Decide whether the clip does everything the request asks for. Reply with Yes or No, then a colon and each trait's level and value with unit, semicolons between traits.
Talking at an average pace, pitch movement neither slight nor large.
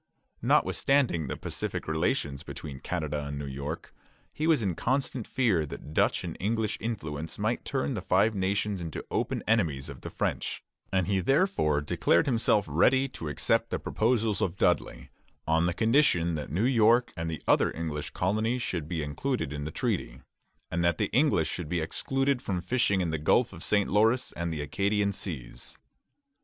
No: average, 175 wpm; wide, 6.5 semitones